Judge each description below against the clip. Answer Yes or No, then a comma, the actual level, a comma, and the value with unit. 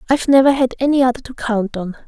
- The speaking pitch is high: Yes, very high, 250 Hz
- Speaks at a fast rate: Yes, fast, 230 wpm